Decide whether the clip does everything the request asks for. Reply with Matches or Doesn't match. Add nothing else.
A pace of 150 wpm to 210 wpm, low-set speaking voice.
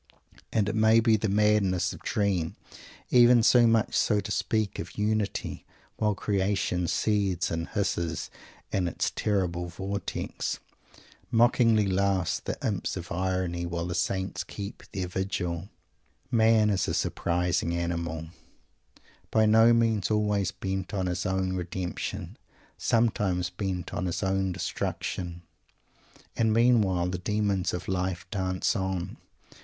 Doesn't match